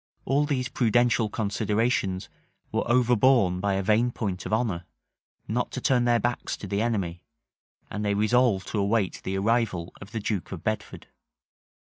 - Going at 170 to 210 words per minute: No, average, 160 wpm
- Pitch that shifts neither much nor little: Yes, average, 3.6 semitones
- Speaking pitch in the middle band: No, low, 110 Hz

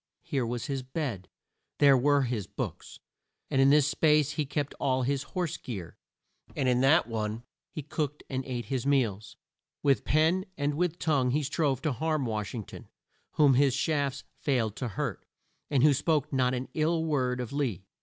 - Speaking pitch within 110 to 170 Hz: Yes, low, 135 Hz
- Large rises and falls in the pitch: No, average, 3.1 semitones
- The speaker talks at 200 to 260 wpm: No, average, 180 wpm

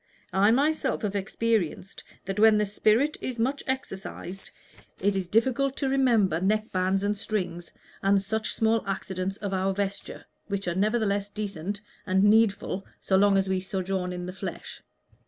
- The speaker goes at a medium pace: Yes, average, 160 wpm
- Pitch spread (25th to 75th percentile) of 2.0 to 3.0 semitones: Yes, narrow, 2.6 semitones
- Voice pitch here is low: No, high, 200 Hz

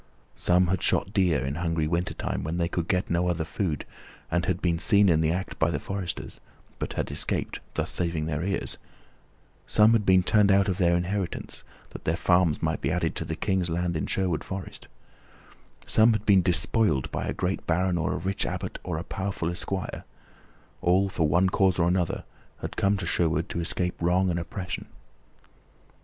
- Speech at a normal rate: Yes, average, 190 wpm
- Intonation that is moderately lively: No, narrow, 2.3 semitones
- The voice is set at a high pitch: No, very low, 90 Hz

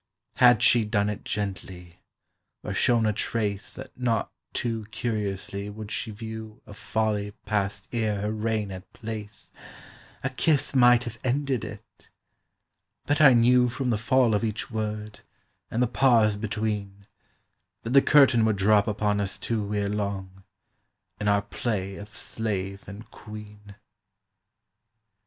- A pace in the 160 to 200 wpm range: No, average, 140 wpm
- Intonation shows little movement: Yes, narrow, 2.3 semitones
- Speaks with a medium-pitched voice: No, low, 105 Hz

